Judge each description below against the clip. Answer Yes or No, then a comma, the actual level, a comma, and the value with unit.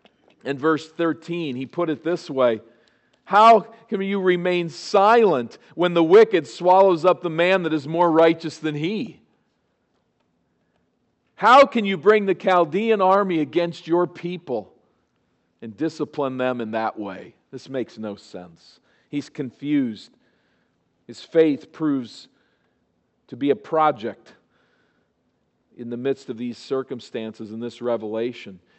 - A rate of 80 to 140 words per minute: Yes, slow, 135 wpm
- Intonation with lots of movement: Yes, wide, 6.2 semitones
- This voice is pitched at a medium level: Yes, medium, 155 Hz